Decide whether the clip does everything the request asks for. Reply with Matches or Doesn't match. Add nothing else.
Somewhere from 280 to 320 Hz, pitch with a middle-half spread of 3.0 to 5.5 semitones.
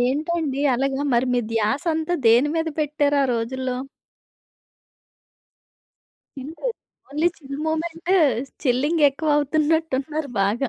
Matches